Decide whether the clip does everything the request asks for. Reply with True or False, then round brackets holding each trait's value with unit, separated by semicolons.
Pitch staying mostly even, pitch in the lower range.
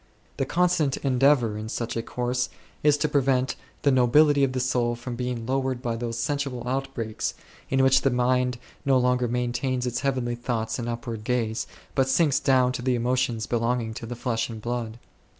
True (2.0 semitones; 125 Hz)